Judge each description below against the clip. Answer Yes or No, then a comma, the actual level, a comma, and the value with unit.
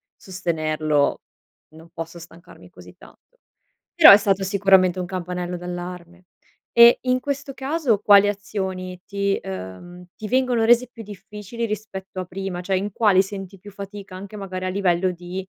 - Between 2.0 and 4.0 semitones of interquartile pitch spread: Yes, average, 2.7 semitones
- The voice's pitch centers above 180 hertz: Yes, high, 190 Hz